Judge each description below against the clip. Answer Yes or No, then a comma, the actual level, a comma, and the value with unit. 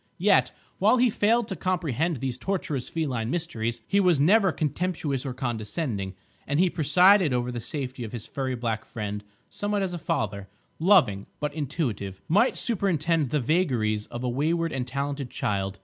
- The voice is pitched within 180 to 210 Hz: No, medium, 140 Hz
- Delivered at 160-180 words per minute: Yes, average, 165 wpm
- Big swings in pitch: Yes, wide, 6.6 semitones